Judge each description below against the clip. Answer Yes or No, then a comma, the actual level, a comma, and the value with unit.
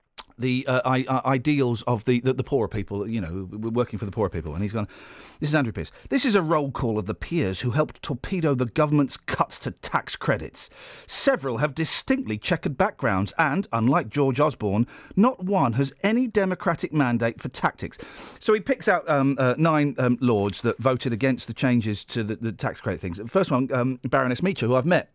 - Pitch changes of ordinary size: Yes, average, 5.0 semitones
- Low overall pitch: Yes, low, 130 Hz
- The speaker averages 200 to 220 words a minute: Yes, fast, 205 wpm